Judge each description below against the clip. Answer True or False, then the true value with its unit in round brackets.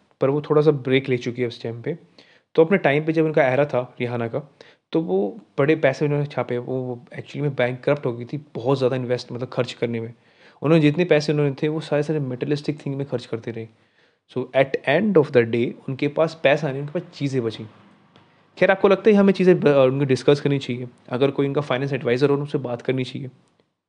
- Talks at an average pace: False (230 wpm)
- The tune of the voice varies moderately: True (3.5 semitones)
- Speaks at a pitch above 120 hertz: True (140 Hz)